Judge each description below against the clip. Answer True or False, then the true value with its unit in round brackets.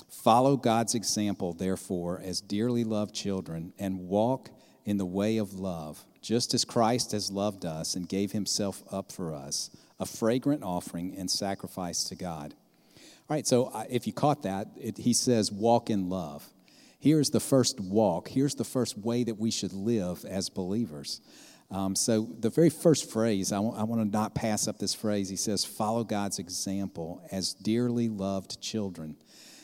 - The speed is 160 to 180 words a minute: True (175 wpm)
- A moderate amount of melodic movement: True (3.5 semitones)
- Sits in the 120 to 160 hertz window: False (105 Hz)